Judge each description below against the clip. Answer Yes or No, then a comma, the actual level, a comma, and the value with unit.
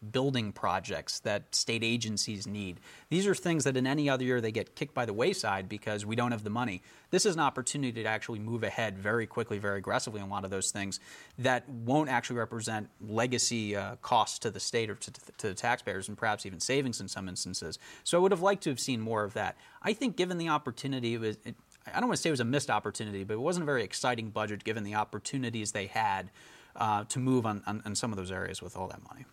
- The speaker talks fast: Yes, fast, 250 wpm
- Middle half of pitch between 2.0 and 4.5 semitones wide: Yes, average, 3.8 semitones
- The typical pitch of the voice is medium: No, low, 115 Hz